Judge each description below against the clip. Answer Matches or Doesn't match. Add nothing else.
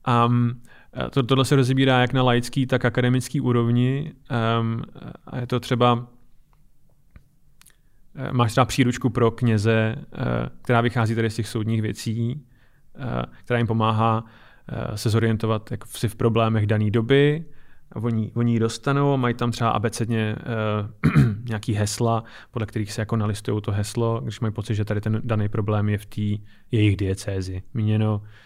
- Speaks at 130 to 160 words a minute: Matches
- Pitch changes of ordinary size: Doesn't match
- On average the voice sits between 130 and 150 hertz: Doesn't match